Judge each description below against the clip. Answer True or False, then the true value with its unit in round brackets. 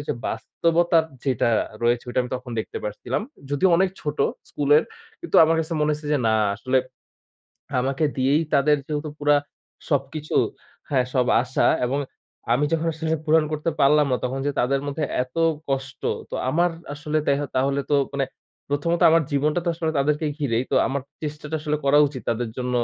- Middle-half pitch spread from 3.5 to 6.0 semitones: False (2.8 semitones)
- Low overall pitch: False (145 Hz)